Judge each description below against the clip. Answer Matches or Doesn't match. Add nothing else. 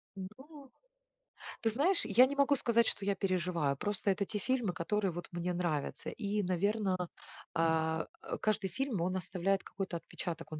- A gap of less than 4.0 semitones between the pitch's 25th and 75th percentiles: Doesn't match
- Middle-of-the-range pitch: Doesn't match